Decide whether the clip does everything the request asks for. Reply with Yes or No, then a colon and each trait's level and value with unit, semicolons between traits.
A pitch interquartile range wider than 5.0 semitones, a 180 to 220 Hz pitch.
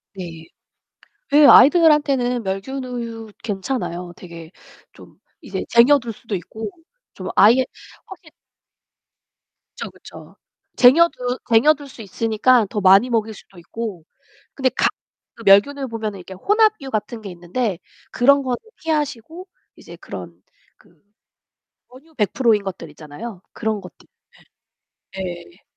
No: wide, 5.5 semitones; high, 230 Hz